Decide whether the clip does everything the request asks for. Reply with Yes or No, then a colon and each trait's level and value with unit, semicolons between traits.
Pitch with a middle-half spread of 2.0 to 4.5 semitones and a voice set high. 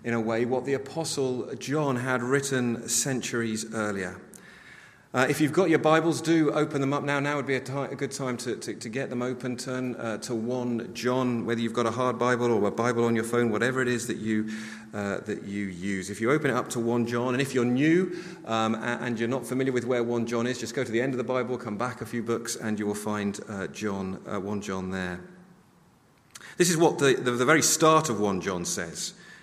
No: average, 3.1 semitones; low, 120 Hz